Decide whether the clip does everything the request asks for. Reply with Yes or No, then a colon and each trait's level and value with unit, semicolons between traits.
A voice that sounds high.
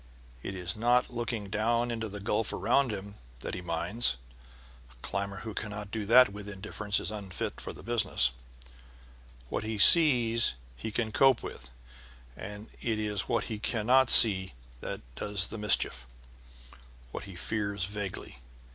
No: low, 105 Hz